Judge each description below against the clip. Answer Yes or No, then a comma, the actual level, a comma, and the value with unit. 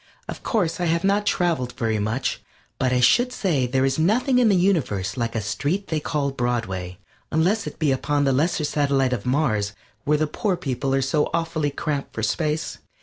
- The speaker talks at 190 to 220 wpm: Yes, average, 200 wpm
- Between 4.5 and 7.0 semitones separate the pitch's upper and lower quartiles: Yes, average, 5.2 semitones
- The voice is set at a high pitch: No, medium, 145 Hz